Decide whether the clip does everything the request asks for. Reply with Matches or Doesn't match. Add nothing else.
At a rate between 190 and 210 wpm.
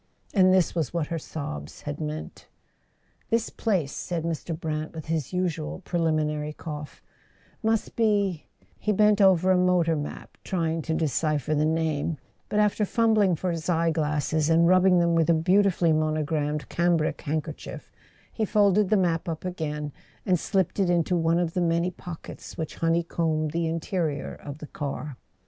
Doesn't match